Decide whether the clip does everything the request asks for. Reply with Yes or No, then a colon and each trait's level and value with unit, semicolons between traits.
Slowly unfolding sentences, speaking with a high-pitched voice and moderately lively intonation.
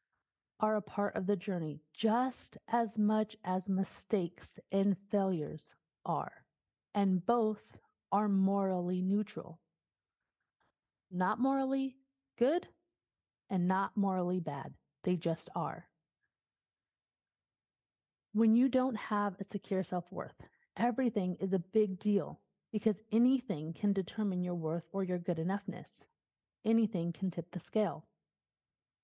Yes: slow, 120 wpm; high, 195 Hz; average, 3.2 semitones